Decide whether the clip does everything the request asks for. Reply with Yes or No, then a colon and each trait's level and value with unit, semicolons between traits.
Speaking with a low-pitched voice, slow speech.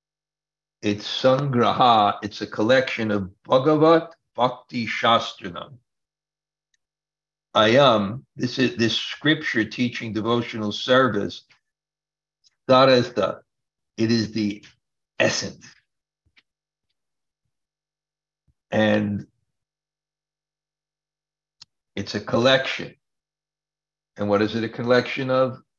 Yes: low, 125 Hz; slow, 75 wpm